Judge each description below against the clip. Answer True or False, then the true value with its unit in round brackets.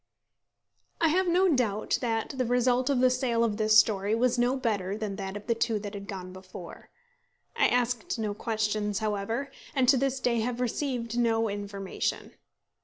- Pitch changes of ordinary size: True (3.3 semitones)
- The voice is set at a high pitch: True (230 Hz)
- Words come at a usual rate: True (180 wpm)